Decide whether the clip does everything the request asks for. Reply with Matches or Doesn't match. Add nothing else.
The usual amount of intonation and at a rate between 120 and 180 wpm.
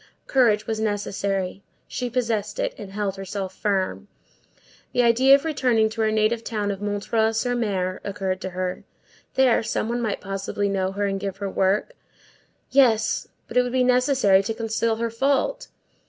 Matches